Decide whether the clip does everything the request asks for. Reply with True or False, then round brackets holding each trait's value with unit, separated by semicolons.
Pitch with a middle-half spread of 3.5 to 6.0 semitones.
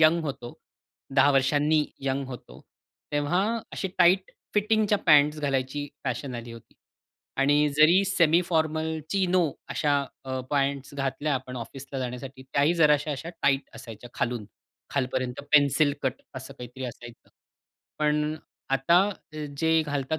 False (3.0 semitones)